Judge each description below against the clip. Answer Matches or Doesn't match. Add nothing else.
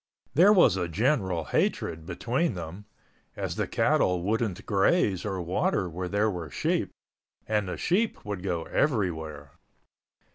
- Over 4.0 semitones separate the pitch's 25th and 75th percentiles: Matches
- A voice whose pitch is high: Doesn't match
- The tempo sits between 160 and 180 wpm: Doesn't match